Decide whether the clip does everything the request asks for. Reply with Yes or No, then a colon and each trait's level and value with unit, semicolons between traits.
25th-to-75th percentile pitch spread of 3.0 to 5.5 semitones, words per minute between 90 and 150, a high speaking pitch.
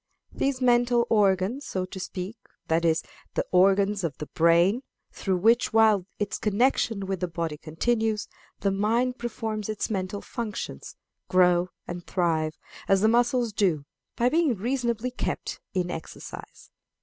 Yes: average, 4.7 semitones; average, 145 wpm; high, 200 Hz